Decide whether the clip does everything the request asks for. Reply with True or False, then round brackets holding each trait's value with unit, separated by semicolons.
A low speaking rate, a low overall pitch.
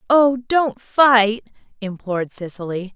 False (100 wpm; 225 Hz)